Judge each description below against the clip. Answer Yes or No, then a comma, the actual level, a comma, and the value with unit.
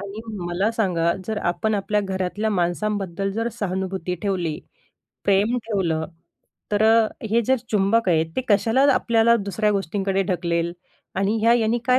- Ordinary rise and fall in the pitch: Yes, average, 3.3 semitones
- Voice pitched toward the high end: Yes, high, 200 Hz